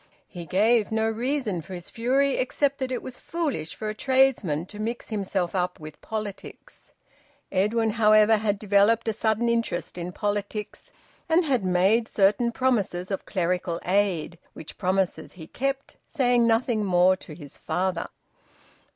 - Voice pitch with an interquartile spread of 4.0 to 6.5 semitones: Yes, average, 4.4 semitones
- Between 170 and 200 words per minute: No, average, 150 wpm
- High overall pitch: Yes, high, 210 Hz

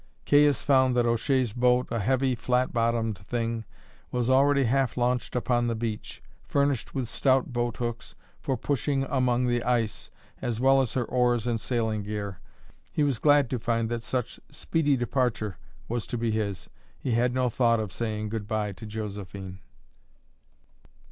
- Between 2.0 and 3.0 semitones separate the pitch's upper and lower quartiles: Yes, narrow, 2.6 semitones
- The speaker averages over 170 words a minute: No, average, 165 wpm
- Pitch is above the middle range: No, low, 120 Hz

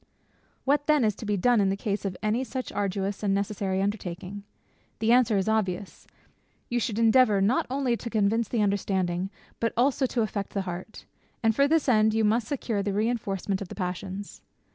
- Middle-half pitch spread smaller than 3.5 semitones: Yes, average, 3.1 semitones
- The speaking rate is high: No, average, 190 wpm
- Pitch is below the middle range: No, high, 210 Hz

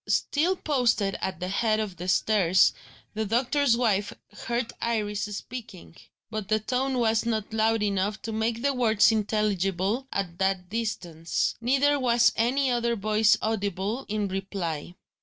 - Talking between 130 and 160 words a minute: Yes, average, 145 wpm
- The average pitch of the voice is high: Yes, high, 215 Hz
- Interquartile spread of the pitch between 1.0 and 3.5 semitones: Yes, average, 3.2 semitones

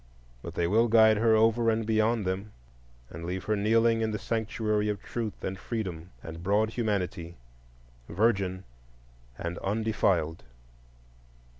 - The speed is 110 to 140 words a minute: Yes, slow, 135 wpm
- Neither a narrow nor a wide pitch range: Yes, average, 3.2 semitones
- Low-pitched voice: Yes, low, 105 Hz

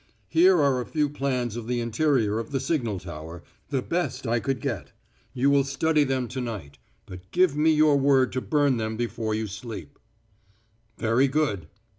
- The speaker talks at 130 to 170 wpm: No, average, 180 wpm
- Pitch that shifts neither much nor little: Yes, average, 4.3 semitones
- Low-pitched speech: Yes, low, 130 Hz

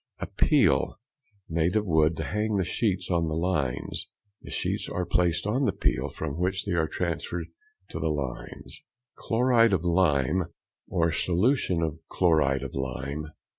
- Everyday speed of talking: Yes, average, 160 wpm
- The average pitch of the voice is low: Yes, very low, 85 Hz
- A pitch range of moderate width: Yes, average, 3.2 semitones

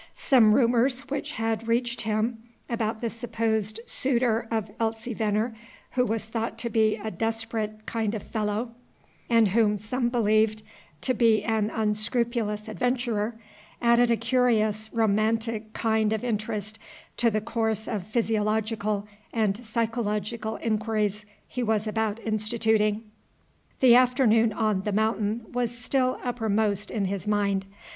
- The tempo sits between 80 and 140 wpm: Yes, slow, 135 wpm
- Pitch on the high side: Yes, high, 220 Hz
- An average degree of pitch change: No, narrow, 1.6 semitones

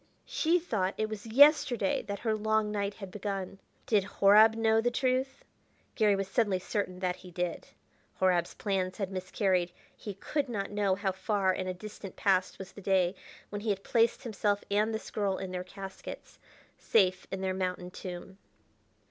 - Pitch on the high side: Yes, high, 200 Hz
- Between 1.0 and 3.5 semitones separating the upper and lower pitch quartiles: Yes, narrow, 2.6 semitones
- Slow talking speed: No, average, 175 wpm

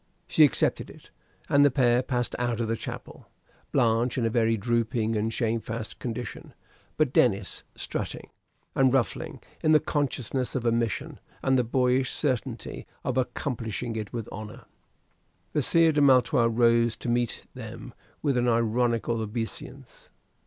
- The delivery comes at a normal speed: Yes, average, 150 wpm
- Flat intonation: Yes, narrow, 2.2 semitones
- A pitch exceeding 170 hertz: No, low, 120 Hz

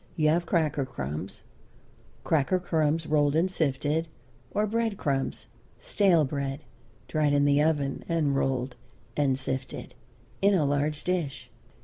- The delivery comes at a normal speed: No, slow, 130 wpm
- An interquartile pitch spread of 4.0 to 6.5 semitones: No, average, 3.1 semitones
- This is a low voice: No, medium, 150 Hz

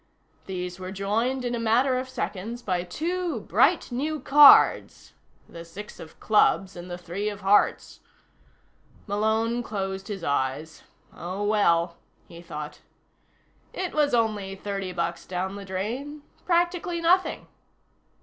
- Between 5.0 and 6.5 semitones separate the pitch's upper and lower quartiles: Yes, wide, 5.4 semitones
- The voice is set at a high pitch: Yes, high, 205 Hz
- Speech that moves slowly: Yes, slow, 130 wpm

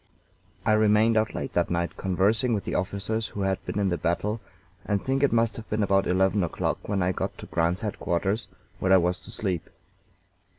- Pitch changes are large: No, average, 2.8 semitones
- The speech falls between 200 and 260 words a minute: Yes, fast, 205 wpm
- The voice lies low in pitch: Yes, low, 100 Hz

